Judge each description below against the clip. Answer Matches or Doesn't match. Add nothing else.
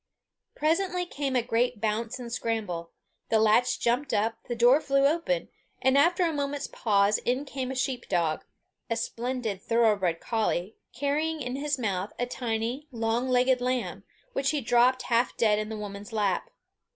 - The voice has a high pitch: Matches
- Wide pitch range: Doesn't match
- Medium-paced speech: Matches